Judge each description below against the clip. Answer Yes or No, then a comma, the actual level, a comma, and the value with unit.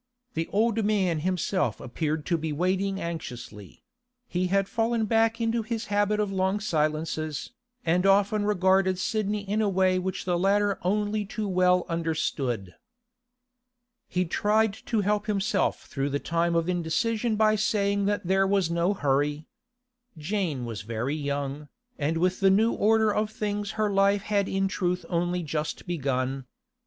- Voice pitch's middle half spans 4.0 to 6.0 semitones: Yes, average, 4.3 semitones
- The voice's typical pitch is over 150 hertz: Yes, high, 190 Hz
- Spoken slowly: No, average, 155 wpm